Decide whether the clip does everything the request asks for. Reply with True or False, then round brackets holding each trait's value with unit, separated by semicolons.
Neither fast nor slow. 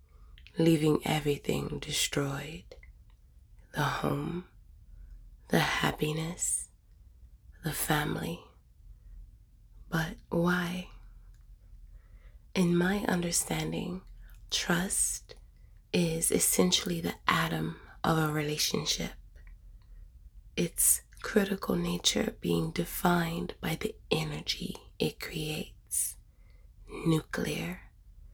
False (70 wpm)